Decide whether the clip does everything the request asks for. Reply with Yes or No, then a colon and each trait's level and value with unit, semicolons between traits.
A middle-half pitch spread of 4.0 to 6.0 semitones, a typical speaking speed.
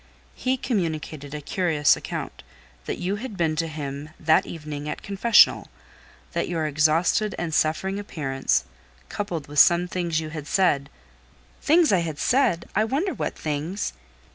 Yes: average, 4.6 semitones; average, 150 wpm